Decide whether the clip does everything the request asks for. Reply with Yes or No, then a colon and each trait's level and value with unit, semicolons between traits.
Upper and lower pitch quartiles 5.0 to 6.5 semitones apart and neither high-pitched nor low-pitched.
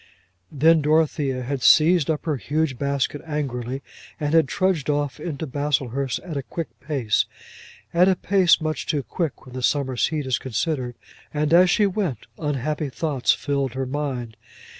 No: average, 3.2 semitones; medium, 145 Hz